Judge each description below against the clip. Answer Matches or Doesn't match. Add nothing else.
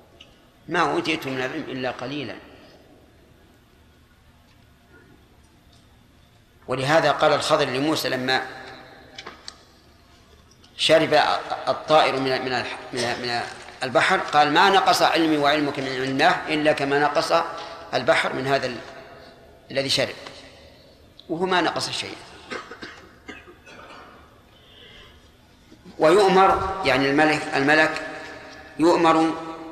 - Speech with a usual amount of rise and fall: Matches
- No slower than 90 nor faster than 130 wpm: Doesn't match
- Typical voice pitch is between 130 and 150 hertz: Matches